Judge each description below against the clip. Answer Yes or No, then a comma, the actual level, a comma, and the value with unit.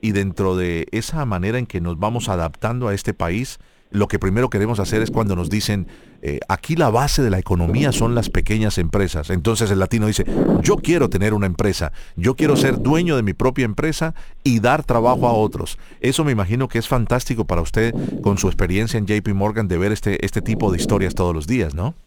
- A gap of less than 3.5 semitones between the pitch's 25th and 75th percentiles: No, average, 4.2 semitones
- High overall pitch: No, low, 110 Hz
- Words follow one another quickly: Yes, fast, 220 wpm